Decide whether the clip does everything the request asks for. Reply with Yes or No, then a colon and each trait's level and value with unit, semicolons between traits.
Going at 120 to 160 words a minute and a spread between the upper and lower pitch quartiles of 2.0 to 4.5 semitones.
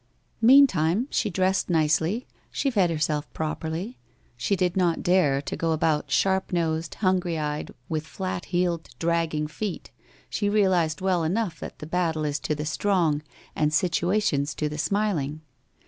Yes: average, 155 wpm; average, 3.4 semitones